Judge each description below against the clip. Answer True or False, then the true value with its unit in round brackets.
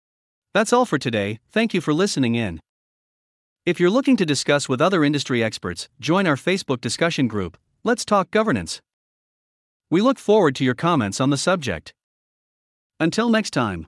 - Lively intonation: True (8.6 semitones)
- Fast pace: False (165 wpm)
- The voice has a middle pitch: True (145 Hz)